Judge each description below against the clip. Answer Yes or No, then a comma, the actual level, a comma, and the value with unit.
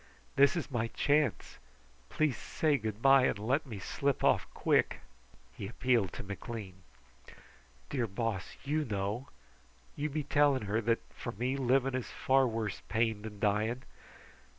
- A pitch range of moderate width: Yes, average, 4.4 semitones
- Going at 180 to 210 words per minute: No, average, 150 wpm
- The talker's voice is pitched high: No, low, 120 Hz